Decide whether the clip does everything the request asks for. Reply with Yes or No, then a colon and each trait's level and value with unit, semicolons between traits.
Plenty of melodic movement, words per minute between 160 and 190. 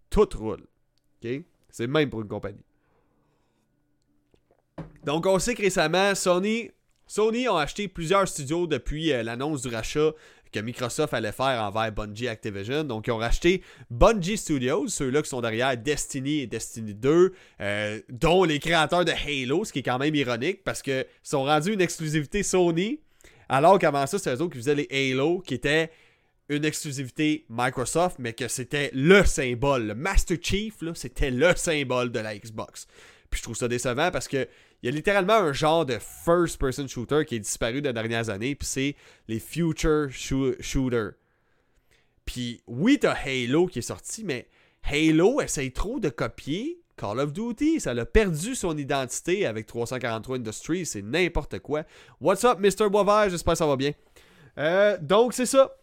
Yes: wide, 6.0 semitones; average, 170 wpm